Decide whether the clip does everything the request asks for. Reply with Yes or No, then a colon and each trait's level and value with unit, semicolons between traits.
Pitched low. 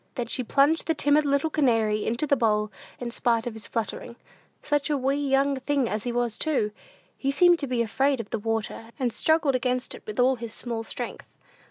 No: very high, 250 Hz